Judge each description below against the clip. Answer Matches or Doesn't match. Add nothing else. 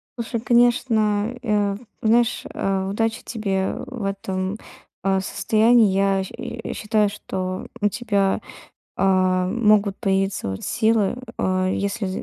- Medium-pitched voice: Doesn't match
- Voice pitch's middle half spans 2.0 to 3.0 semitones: Matches